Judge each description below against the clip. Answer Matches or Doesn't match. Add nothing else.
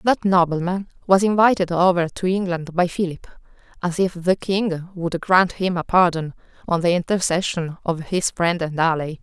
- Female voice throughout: Matches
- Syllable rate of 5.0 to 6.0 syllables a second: Doesn't match